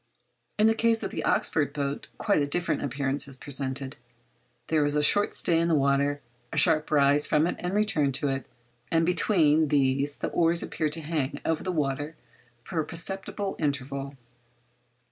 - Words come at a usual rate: Yes, average, 170 wpm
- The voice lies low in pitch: No, medium, 145 Hz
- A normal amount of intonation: Yes, average, 3.2 semitones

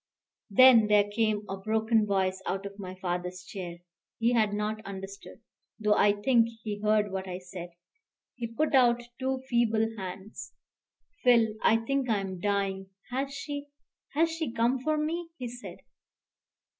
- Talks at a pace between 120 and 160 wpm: Yes, average, 155 wpm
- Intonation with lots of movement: No, average, 3.8 semitones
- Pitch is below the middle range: No, high, 215 Hz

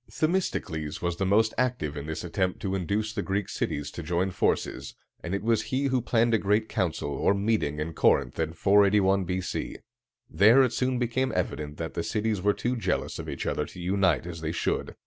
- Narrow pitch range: No, average, 5.0 semitones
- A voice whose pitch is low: Yes, low, 100 Hz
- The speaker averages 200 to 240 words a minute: Yes, fast, 205 wpm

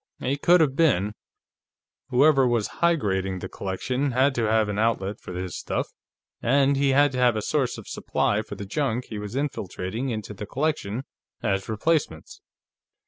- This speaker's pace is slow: No, average, 170 wpm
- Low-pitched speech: Yes, low, 120 Hz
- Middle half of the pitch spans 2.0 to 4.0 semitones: No, average, 5.3 semitones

